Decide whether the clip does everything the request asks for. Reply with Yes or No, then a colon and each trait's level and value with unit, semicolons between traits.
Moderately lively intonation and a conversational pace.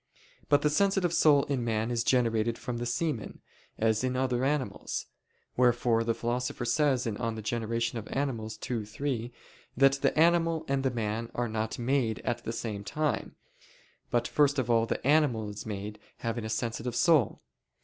Yes: average, 3.3 semitones; average, 165 wpm